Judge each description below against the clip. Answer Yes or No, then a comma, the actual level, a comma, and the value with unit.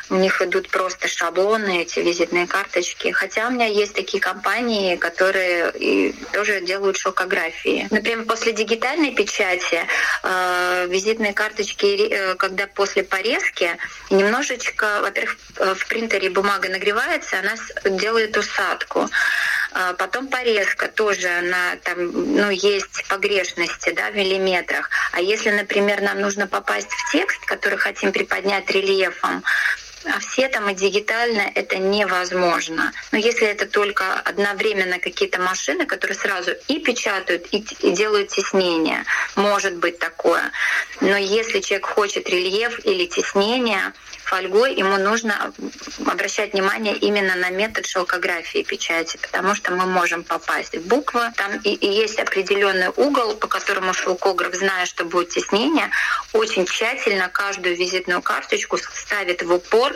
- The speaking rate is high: No, average, 130 wpm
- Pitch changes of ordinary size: Yes, average, 3.3 semitones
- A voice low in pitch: No, high, 200 Hz